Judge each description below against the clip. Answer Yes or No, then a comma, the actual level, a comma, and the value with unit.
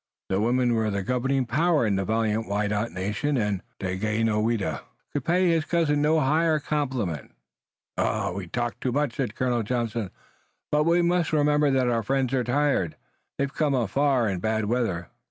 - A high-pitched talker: No, low, 120 Hz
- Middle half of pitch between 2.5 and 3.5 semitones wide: No, wide, 5.5 semitones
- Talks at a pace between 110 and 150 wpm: No, average, 160 wpm